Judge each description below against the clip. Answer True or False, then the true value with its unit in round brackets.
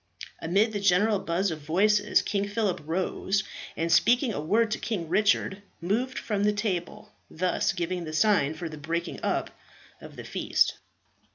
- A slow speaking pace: False (165 wpm)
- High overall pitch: True (195 Hz)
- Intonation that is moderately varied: True (3.9 semitones)